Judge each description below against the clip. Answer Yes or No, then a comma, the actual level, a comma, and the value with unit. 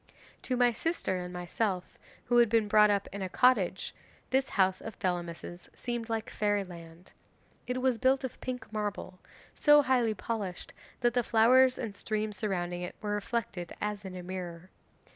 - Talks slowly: No, average, 165 wpm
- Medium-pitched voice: No, high, 210 Hz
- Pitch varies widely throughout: No, average, 4.6 semitones